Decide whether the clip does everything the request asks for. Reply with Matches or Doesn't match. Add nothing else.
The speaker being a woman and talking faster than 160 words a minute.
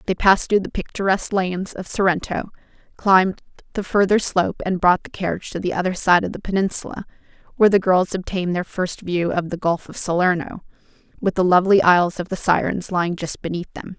Matches